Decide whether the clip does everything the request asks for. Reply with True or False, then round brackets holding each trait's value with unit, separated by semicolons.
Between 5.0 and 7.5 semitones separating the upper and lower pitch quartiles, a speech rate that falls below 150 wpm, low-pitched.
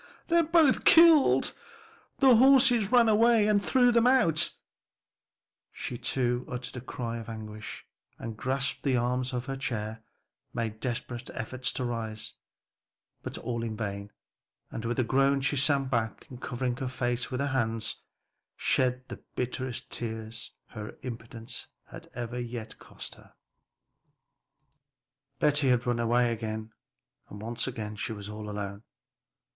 False (3.3 semitones; 140 wpm; 125 Hz)